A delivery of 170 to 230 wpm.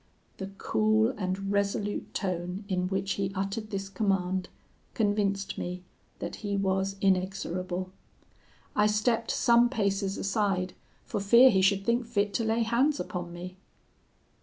No: slow, 135 wpm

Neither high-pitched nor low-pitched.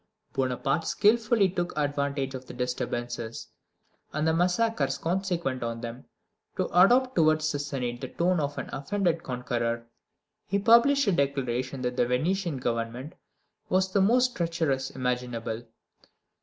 Yes: medium, 145 Hz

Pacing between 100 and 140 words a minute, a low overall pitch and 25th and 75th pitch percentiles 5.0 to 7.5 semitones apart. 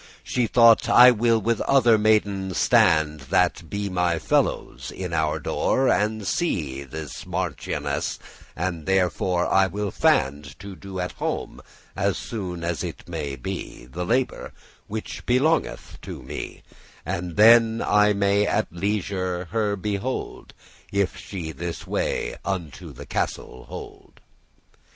No: slow, 135 wpm; very low, 95 Hz; average, 4.3 semitones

